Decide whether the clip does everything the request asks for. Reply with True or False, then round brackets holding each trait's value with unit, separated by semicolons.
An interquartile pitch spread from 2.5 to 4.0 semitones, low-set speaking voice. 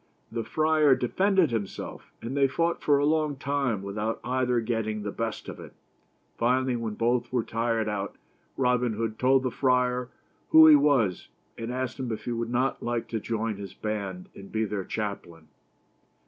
True (3.3 semitones; 120 Hz)